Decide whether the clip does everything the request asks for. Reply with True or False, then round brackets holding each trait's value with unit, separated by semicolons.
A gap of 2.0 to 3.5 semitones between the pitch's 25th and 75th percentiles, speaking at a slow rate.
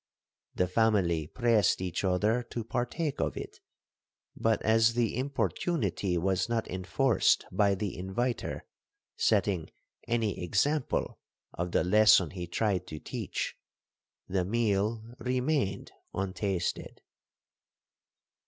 False (4.2 semitones; 105 wpm)